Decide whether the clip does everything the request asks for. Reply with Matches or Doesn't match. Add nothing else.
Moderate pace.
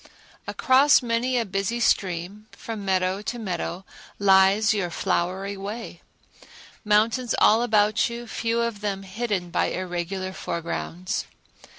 Doesn't match